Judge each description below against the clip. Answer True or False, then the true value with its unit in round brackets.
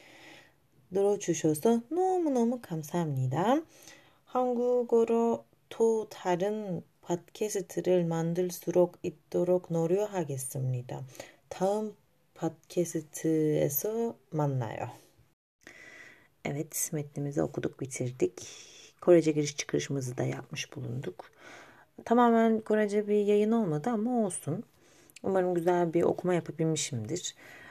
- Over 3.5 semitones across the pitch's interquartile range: True (5.4 semitones)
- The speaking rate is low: True (65 wpm)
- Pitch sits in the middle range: True (175 Hz)